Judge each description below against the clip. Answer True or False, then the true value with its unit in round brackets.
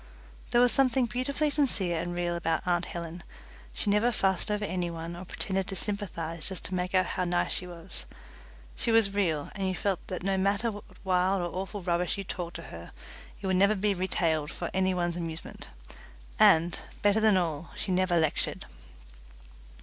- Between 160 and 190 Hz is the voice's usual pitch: True (185 Hz)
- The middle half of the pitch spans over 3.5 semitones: False (2.7 semitones)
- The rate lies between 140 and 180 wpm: False (190 wpm)